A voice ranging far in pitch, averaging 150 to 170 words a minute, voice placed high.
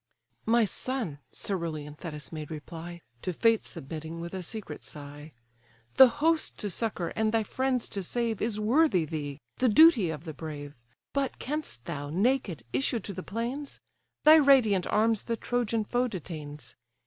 Yes: wide, 7.2 semitones; average, 160 wpm; high, 195 Hz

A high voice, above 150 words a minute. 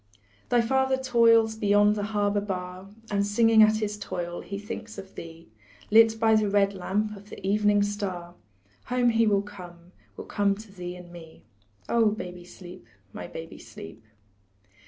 Yes: high, 205 Hz; average, 165 wpm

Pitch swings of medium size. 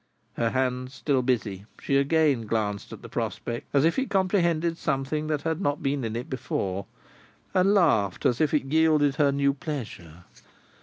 Yes: average, 4.9 semitones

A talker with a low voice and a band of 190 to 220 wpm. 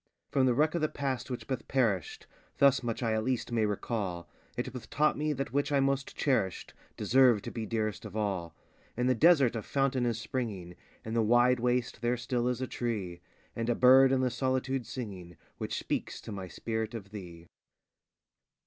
Yes: low, 120 Hz; average, 200 wpm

